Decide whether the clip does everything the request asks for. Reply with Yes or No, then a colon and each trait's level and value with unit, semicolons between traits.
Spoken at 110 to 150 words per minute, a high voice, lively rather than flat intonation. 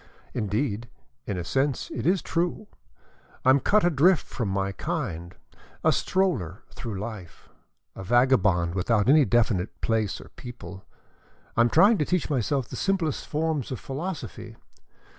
No: average, 145 wpm; low, 120 Hz; wide, 7.4 semitones